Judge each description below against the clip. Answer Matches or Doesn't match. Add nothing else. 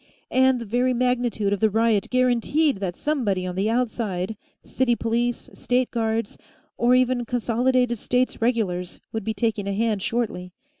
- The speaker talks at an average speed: Matches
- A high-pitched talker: Matches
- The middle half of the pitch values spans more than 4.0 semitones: Doesn't match